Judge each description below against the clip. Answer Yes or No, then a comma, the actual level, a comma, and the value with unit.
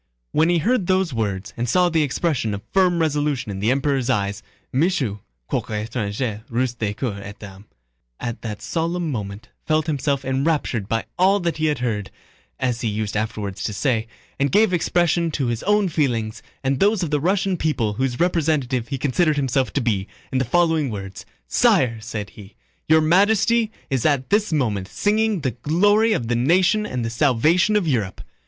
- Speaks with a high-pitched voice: No, low, 135 Hz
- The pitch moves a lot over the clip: Yes, wide, 7.2 semitones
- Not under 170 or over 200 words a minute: Yes, average, 180 wpm